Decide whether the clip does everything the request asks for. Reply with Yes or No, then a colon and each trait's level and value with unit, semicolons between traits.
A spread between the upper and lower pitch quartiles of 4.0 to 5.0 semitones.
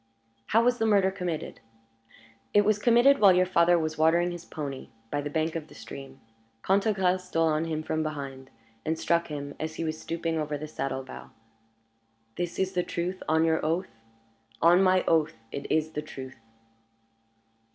No: average, 3.1 semitones